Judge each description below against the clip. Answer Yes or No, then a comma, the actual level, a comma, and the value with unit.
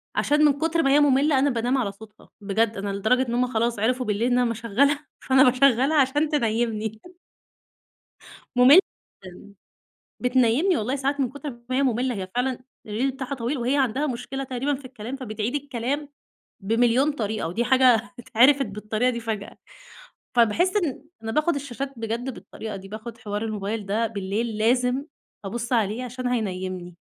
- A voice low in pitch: No, high, 245 Hz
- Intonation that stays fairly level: No, average, 3.6 semitones